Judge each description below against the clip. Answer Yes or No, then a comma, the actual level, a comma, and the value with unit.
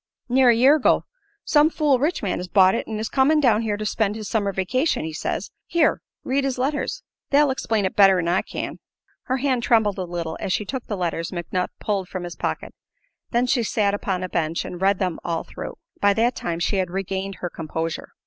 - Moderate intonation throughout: No, wide, 5.7 semitones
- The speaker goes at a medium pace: No, fast, 225 wpm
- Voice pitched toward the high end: Yes, high, 205 Hz